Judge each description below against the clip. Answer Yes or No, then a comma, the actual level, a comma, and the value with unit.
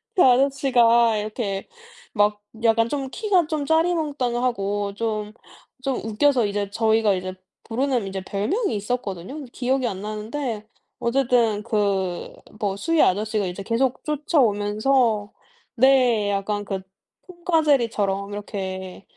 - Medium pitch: No, high, 225 Hz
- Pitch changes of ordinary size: Yes, average, 4.5 semitones